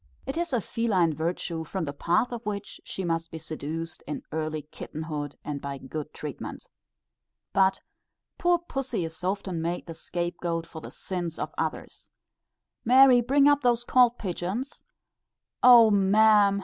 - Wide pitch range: Yes, wide, 6.4 semitones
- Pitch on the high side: No, medium, 180 Hz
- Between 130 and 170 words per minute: Yes, average, 160 wpm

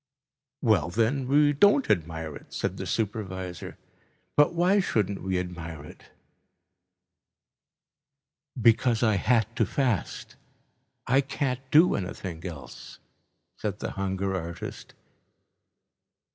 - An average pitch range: No, wide, 6.9 semitones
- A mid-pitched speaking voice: No, low, 105 Hz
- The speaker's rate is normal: No, slow, 105 wpm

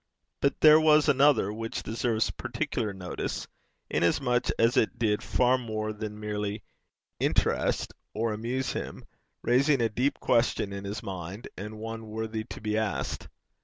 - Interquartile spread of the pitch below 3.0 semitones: Yes, narrow, 2.6 semitones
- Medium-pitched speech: No, low, 110 Hz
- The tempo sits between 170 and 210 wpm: No, average, 145 wpm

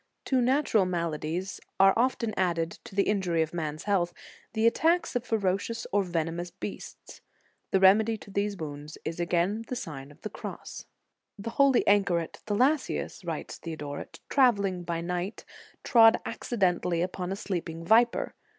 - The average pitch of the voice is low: No, high, 190 Hz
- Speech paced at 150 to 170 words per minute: Yes, average, 155 wpm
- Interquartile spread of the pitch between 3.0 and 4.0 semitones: No, average, 4.7 semitones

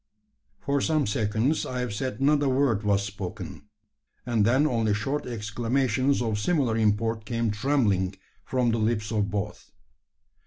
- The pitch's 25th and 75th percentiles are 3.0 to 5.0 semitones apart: Yes, average, 3.9 semitones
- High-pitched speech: No, low, 115 Hz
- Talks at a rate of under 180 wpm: Yes, average, 150 wpm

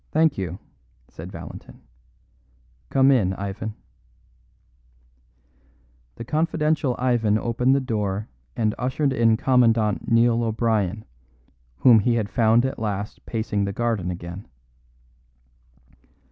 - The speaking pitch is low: Yes, low, 115 Hz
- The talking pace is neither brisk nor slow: No, slow, 105 wpm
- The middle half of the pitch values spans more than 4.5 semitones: No, average, 3.4 semitones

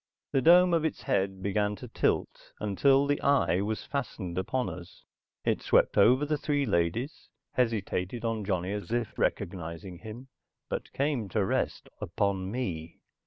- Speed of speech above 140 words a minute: Yes, average, 155 wpm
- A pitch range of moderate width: No, wide, 6.1 semitones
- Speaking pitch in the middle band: No, low, 110 Hz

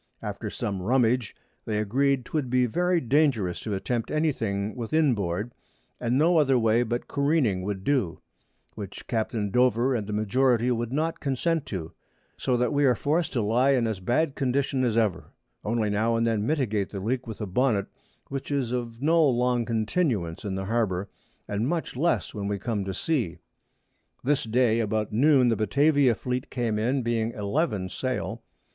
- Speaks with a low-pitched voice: Yes, low, 120 Hz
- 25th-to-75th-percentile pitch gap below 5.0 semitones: Yes, average, 4.2 semitones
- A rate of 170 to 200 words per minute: Yes, average, 175 wpm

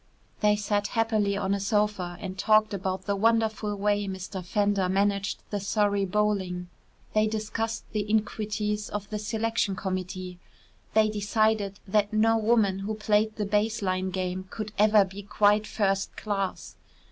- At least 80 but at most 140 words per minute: No, average, 150 wpm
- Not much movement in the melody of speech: Yes, narrow, 1.8 semitones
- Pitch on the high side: Yes, high, 205 Hz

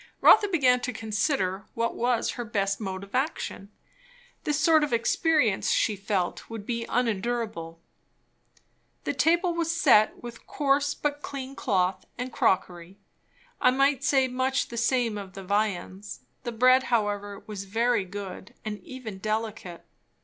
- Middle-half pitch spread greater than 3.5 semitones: Yes, average, 4.6 semitones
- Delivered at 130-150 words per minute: Yes, average, 145 wpm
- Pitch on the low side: No, high, 230 Hz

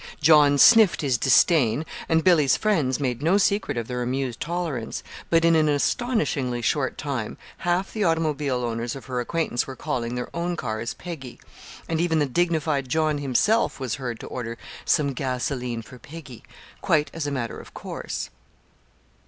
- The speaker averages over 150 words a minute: Yes, average, 165 wpm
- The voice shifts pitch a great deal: No, average, 4.9 semitones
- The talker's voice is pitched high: No, medium, 145 Hz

